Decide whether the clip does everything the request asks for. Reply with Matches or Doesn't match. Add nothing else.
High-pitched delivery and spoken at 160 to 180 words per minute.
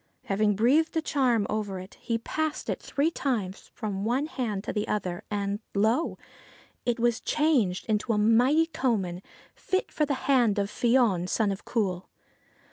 Matches